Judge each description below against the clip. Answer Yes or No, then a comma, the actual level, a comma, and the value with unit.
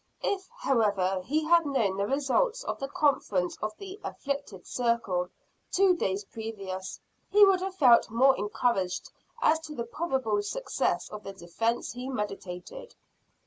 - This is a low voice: No, high, 235 Hz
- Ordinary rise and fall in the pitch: No, wide, 7.8 semitones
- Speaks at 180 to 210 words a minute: No, average, 145 wpm